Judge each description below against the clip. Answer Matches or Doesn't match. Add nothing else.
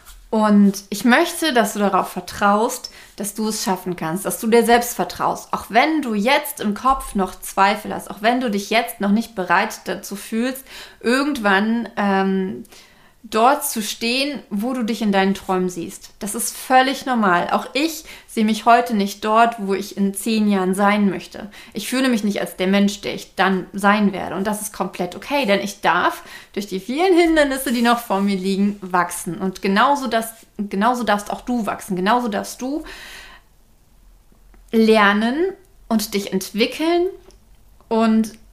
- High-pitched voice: Matches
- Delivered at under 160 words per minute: Doesn't match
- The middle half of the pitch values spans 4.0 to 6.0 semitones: Doesn't match